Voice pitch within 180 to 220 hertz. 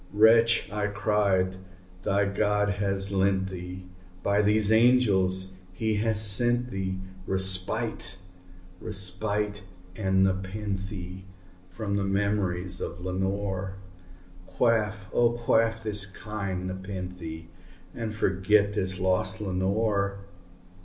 No: low, 100 Hz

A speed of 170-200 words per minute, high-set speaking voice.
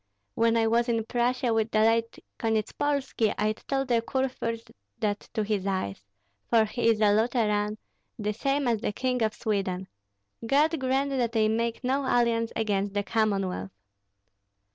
No: average, 160 wpm; high, 225 Hz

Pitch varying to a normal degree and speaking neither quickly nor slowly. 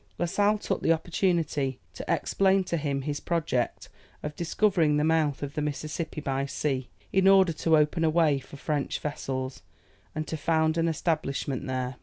Yes: average, 3.0 semitones; average, 175 wpm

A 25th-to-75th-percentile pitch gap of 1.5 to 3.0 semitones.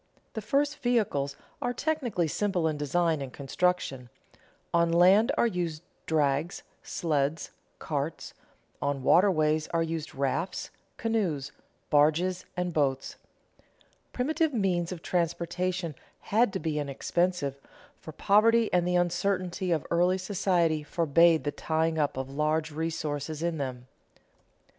No: average, 3.6 semitones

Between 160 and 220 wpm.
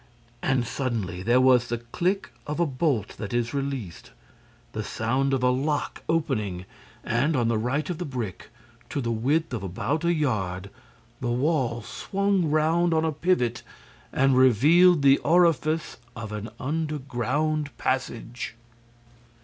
No: average, 145 wpm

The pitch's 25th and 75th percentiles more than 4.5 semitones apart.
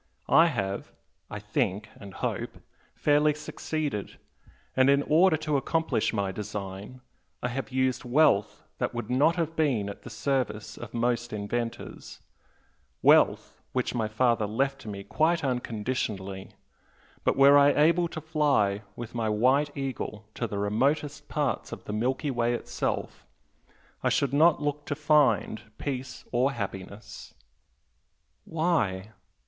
Yes: wide, 5.5 semitones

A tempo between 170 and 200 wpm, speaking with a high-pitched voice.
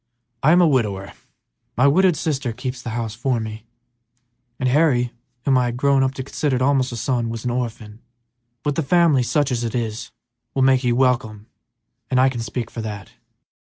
No: average, 180 wpm; low, 125 Hz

